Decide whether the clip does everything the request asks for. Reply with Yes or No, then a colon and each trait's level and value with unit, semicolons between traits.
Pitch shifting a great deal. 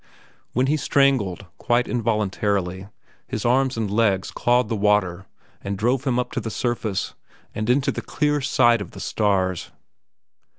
No: average, 3.9 semitones